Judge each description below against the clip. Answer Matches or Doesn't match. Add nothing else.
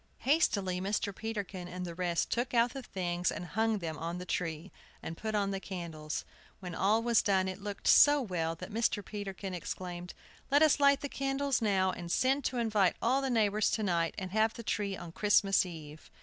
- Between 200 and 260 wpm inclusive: Matches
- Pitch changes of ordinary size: Matches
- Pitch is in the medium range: Doesn't match